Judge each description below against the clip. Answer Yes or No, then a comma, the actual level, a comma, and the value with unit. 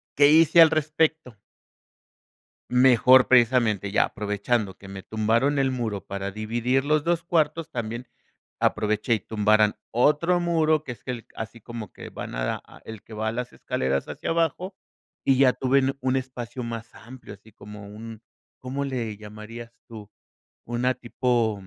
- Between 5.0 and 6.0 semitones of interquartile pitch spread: No, average, 3.9 semitones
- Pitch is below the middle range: Yes, low, 120 Hz